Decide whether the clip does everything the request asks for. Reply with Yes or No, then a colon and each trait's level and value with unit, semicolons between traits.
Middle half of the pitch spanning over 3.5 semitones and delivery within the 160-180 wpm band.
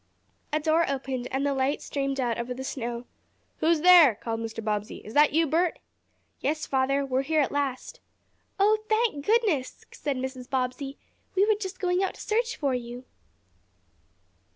Yes: average, 4.6 semitones; average, 175 wpm